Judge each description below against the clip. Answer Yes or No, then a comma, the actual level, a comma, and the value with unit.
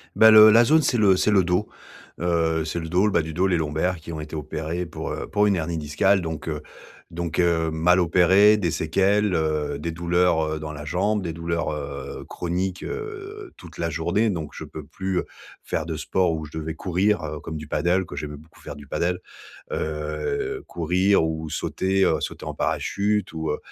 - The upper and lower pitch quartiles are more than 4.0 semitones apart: No, average, 3.4 semitones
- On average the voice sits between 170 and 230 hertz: No, very low, 85 Hz